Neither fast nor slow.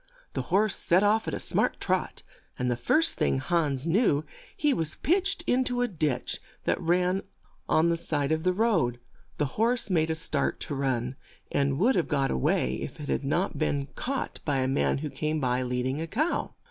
No: fast, 210 wpm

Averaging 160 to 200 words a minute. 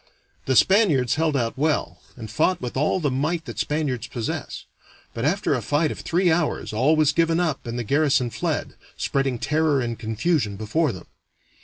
Yes: average, 180 wpm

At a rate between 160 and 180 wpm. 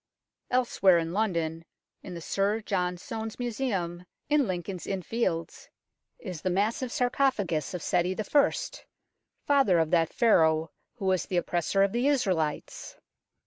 No: average, 140 wpm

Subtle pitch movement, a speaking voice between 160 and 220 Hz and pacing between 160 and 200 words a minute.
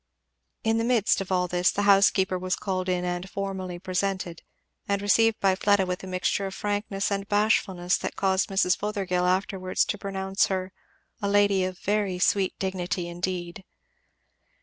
Yes: narrow, 1.6 semitones; high, 190 Hz; average, 170 wpm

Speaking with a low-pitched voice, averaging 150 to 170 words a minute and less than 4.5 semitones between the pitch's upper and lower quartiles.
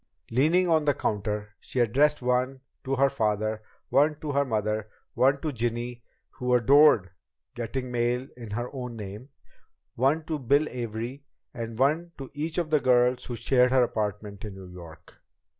Yes: low, 125 Hz; average, 165 wpm; average, 4.1 semitones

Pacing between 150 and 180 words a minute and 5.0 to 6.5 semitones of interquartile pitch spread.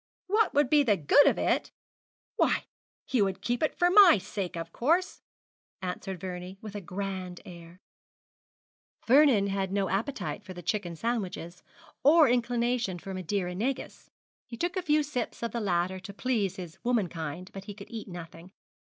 Yes: average, 170 wpm; average, 5.3 semitones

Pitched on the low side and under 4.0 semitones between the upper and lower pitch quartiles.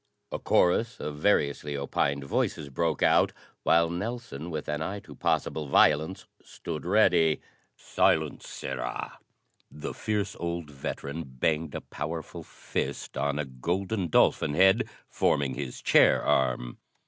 Yes: very low, 80 Hz; average, 3.6 semitones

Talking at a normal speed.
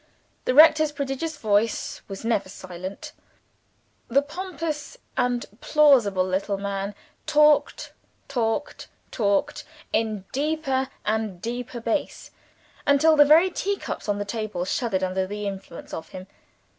No: slow, 120 wpm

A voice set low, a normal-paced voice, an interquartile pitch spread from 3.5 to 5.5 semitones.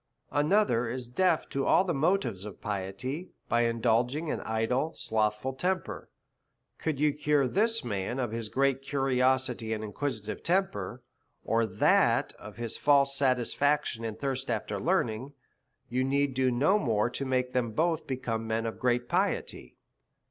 Yes: low, 125 Hz; average, 150 wpm; average, 4.2 semitones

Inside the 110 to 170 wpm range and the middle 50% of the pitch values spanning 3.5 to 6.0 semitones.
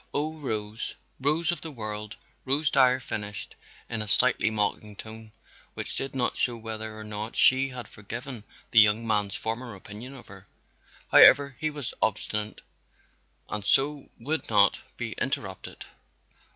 Yes: average, 150 wpm; average, 4.1 semitones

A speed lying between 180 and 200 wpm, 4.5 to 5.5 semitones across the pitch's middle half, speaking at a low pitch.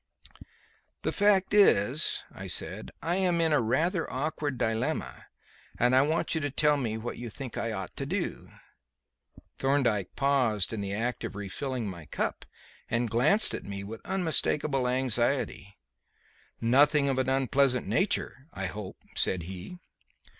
No: average, 150 wpm; average, 5.1 semitones; low, 130 Hz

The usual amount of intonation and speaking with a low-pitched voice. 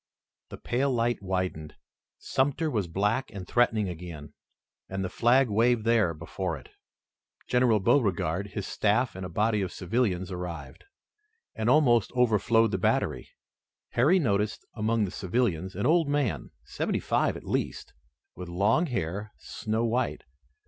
Yes: average, 4.6 semitones; low, 105 Hz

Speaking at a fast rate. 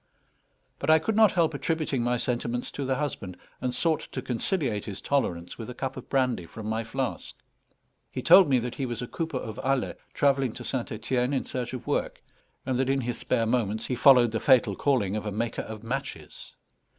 Yes: fast, 210 wpm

